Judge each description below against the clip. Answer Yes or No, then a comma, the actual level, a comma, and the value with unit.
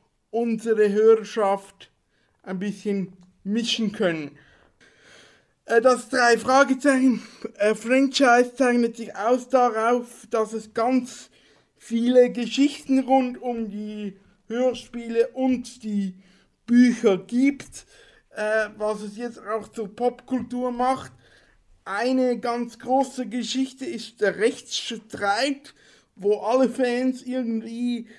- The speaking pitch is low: No, high, 235 Hz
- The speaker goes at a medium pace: No, slow, 100 wpm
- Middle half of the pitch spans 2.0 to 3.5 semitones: Yes, average, 2.8 semitones